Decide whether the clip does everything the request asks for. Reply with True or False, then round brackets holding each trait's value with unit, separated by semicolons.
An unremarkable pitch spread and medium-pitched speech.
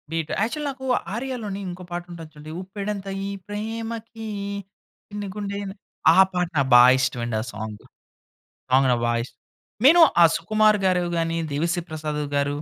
False (5.9 semitones; 180 Hz)